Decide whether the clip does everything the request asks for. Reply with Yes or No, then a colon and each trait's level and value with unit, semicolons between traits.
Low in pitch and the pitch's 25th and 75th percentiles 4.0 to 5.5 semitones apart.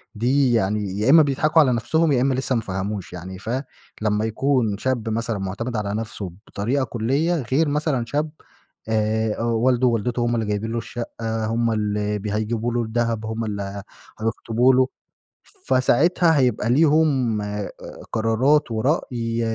No: low, 115 Hz; average, 3.4 semitones